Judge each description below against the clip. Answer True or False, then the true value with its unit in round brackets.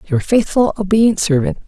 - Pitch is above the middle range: True (225 Hz)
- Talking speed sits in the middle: True (145 wpm)